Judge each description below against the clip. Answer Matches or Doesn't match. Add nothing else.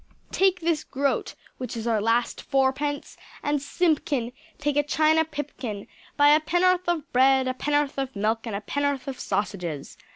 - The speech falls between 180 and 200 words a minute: Doesn't match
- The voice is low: Doesn't match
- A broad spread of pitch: Doesn't match